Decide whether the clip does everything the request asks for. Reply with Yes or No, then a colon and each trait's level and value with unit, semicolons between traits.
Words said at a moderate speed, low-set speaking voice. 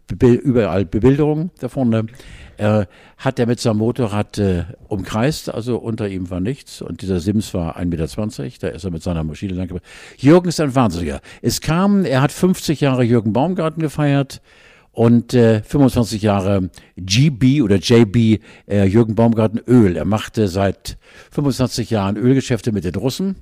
Yes: average, 155 wpm; low, 115 Hz